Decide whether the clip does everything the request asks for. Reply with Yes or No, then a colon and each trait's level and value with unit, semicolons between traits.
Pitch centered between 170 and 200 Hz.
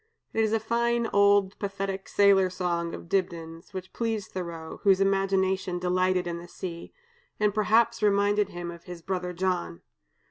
Yes: high, 190 Hz